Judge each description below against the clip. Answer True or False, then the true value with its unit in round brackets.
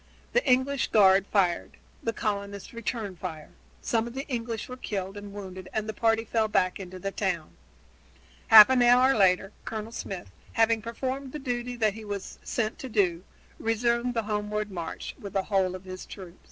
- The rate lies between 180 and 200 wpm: True (185 wpm)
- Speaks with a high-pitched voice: True (215 Hz)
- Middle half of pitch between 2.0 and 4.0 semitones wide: True (3.5 semitones)